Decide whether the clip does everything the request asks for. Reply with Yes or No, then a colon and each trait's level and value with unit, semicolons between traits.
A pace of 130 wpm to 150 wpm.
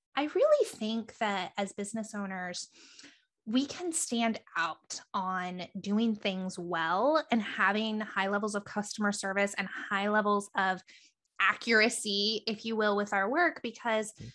Yes: average, 140 wpm